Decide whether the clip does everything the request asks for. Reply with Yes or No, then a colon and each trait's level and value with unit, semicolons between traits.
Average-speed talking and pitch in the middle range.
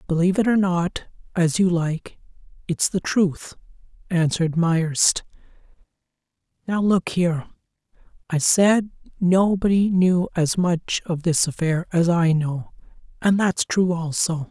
No: slow, 120 wpm; medium, 175 Hz